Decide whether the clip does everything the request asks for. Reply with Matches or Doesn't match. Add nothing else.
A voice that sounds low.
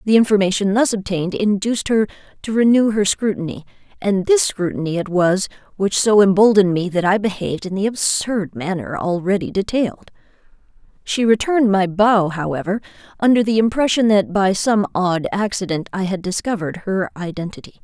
Doesn't match